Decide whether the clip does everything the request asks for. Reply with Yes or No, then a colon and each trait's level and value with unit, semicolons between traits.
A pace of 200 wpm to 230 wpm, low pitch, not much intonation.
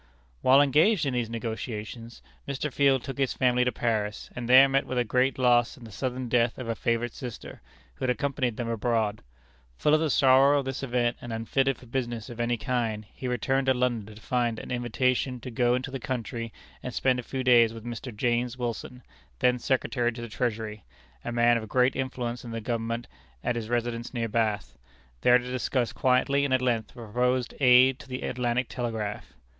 Yes: fast, 205 wpm; low, 125 Hz; narrow, 1.9 semitones